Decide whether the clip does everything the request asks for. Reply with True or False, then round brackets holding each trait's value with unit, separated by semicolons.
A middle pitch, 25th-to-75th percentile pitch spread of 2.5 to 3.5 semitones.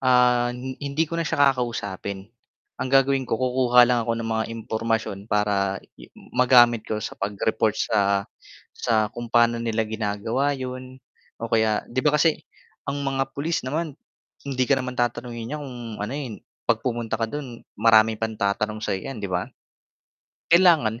False (120 Hz; 3.1 semitones)